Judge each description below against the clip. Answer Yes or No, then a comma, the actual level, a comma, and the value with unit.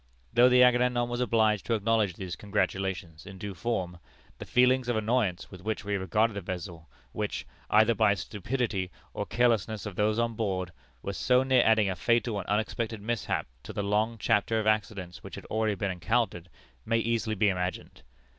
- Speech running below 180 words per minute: No, average, 185 wpm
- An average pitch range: Yes, average, 3.3 semitones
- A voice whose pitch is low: Yes, low, 105 Hz